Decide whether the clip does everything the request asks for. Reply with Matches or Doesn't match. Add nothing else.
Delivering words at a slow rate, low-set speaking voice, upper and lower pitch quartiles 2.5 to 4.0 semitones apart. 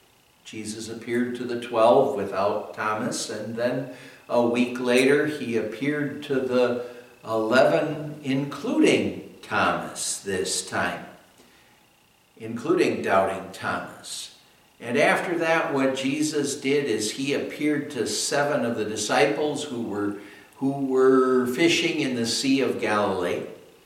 Matches